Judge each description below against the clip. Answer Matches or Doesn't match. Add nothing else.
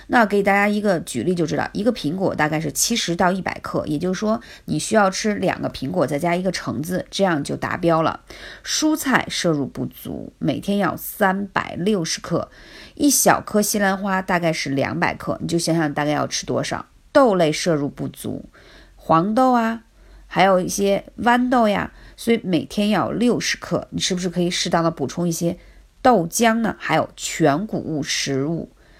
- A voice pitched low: Doesn't match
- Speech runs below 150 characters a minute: Doesn't match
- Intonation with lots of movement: Doesn't match